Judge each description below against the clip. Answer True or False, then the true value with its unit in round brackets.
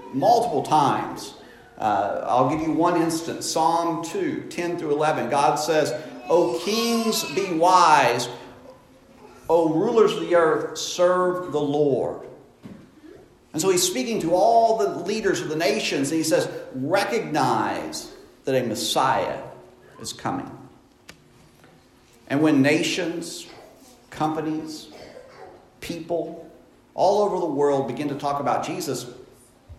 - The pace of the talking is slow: True (125 wpm)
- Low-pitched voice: False (165 Hz)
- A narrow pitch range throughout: False (3.1 semitones)